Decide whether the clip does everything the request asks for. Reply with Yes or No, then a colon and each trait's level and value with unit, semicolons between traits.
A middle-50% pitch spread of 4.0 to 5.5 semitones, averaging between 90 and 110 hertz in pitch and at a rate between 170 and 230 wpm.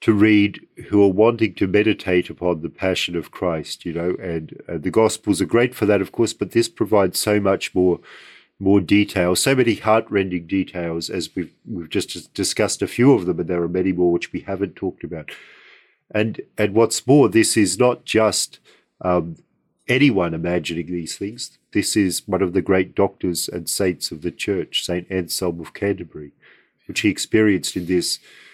No: average, 3.3 semitones; very low, 95 Hz; average, 190 wpm